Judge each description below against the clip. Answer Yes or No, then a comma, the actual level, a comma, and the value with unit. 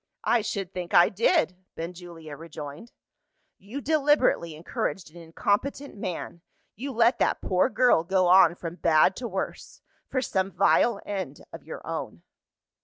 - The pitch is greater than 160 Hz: Yes, high, 190 Hz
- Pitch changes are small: No, wide, 5.6 semitones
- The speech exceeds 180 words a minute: No, average, 145 wpm